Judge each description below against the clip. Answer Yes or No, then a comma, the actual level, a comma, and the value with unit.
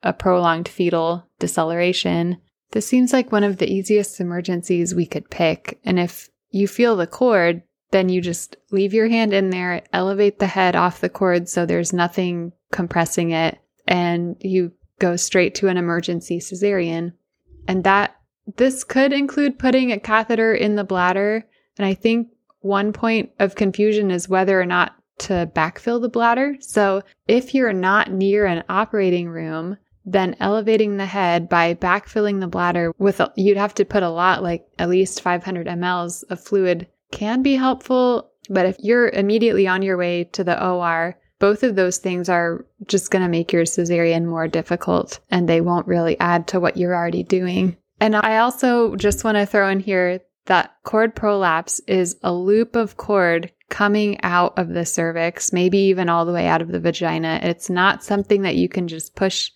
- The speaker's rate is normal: Yes, average, 180 wpm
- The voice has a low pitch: No, medium, 185 Hz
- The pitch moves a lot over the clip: No, average, 3.1 semitones